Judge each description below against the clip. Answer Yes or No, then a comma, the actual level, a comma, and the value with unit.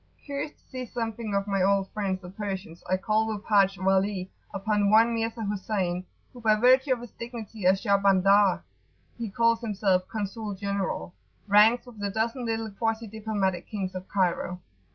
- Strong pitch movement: No, average, 2.7 semitones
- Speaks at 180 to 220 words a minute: No, average, 170 wpm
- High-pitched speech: Yes, high, 205 Hz